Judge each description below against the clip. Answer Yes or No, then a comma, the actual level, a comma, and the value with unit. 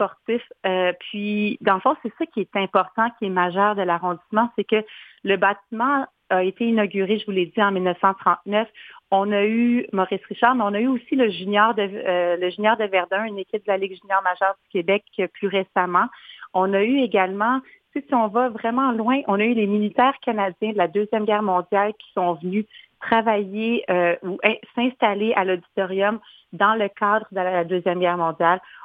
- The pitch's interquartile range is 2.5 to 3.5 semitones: Yes, average, 3.2 semitones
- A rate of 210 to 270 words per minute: No, average, 200 wpm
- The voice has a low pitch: No, high, 205 Hz